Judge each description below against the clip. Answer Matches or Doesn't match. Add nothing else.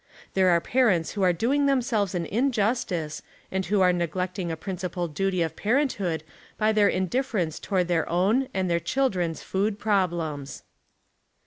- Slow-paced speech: Doesn't match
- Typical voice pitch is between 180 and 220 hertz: Matches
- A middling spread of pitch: Matches